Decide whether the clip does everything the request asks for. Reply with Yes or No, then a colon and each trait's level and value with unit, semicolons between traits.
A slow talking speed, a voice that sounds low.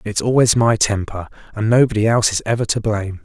No: fast, 205 wpm; low, 110 Hz